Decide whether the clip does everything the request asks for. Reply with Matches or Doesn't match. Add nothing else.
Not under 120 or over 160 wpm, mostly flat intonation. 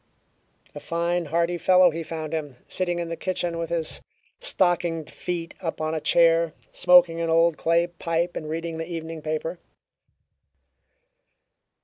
Matches